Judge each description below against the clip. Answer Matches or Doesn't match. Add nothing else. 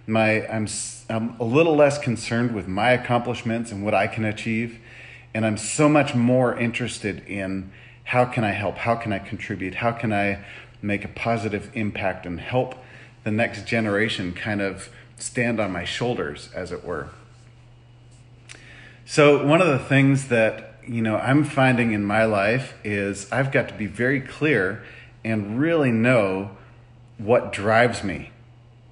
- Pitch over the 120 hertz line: Doesn't match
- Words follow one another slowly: Doesn't match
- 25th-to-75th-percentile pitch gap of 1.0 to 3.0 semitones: Matches